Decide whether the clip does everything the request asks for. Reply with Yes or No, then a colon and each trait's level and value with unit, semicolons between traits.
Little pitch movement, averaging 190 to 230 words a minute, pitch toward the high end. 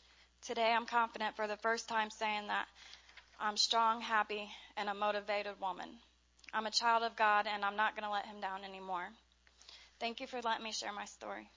Yes: narrow, 1.8 semitones; average, 195 wpm; high, 215 Hz